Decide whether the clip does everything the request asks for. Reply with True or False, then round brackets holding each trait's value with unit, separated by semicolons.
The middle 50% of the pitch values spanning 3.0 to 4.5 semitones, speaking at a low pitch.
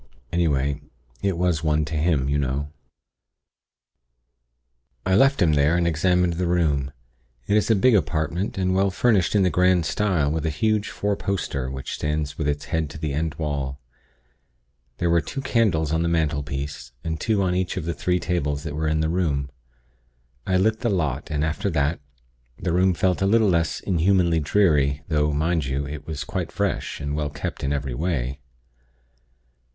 True (4.0 semitones; 80 Hz)